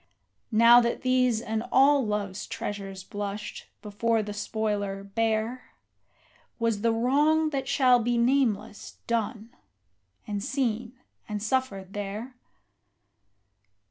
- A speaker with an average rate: No, slow, 110 wpm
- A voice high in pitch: Yes, high, 225 Hz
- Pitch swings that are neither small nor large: Yes, average, 3.4 semitones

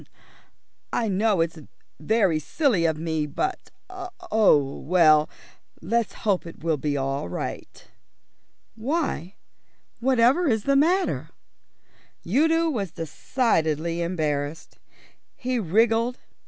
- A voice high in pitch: Yes, high, 195 Hz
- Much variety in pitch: Yes, wide, 7.9 semitones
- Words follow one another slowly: Yes, slow, 100 wpm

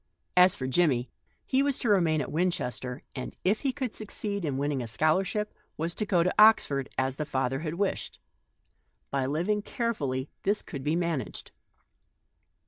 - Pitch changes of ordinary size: No, wide, 7.0 semitones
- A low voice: No, medium, 165 Hz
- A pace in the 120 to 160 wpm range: No, average, 170 wpm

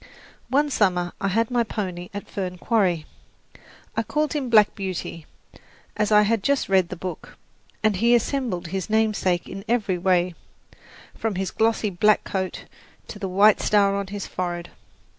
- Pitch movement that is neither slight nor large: Yes, average, 3.3 semitones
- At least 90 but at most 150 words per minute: No, average, 160 wpm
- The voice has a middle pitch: No, high, 200 Hz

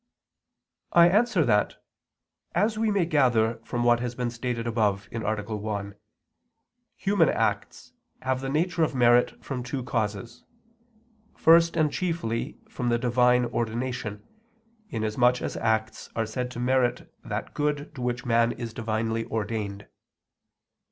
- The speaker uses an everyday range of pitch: Yes, average, 3.1 semitones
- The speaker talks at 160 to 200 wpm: No, slow, 135 wpm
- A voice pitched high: No, low, 120 Hz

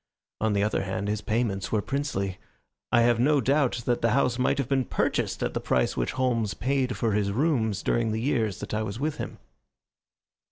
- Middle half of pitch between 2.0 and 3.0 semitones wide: No, average, 3.8 semitones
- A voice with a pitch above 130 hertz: No, low, 115 Hz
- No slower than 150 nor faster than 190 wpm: No, fast, 205 wpm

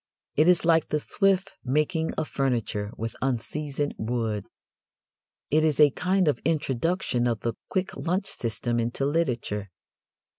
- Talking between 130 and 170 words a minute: Yes, average, 140 wpm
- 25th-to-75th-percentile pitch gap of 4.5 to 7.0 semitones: Yes, wide, 5.6 semitones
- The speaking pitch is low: No, medium, 145 Hz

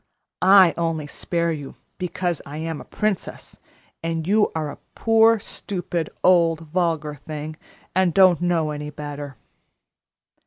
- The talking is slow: Yes, slow, 130 wpm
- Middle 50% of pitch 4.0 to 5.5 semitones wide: No, average, 3.2 semitones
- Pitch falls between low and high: Yes, medium, 165 Hz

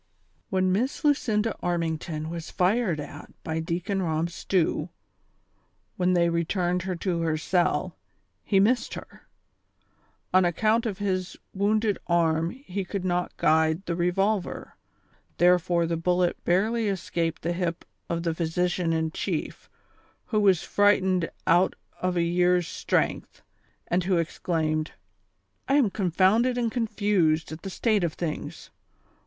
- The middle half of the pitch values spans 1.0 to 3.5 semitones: Yes, average, 3.0 semitones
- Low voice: No, medium, 180 Hz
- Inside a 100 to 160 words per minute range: Yes, average, 140 wpm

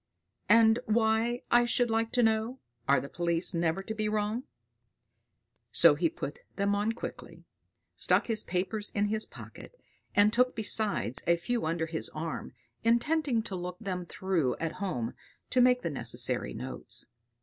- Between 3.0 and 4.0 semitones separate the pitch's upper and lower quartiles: No, average, 4.8 semitones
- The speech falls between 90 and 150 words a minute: No, average, 160 wpm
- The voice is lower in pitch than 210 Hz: No, high, 215 Hz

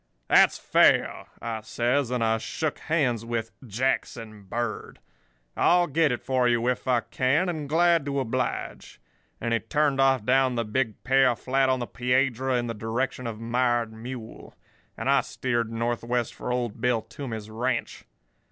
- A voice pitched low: Yes, low, 125 Hz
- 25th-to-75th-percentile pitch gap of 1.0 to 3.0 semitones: Yes, narrow, 2.5 semitones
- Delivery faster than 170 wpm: No, average, 160 wpm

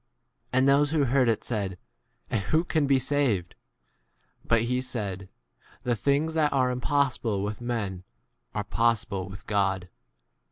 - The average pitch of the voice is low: Yes, low, 120 Hz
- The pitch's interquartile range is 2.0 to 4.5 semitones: No, wide, 5.4 semitones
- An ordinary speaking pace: Yes, average, 155 wpm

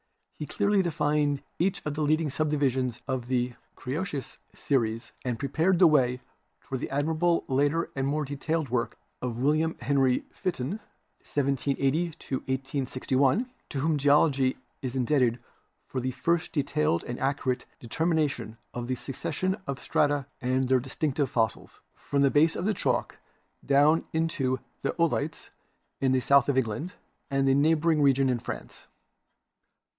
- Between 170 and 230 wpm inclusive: No, average, 150 wpm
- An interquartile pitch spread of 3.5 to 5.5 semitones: No, average, 3.0 semitones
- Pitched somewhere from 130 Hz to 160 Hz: Yes, medium, 140 Hz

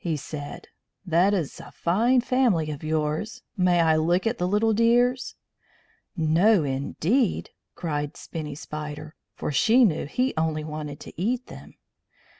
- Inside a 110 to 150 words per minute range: Yes, average, 145 wpm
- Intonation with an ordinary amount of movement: No, wide, 6.4 semitones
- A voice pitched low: No, medium, 170 Hz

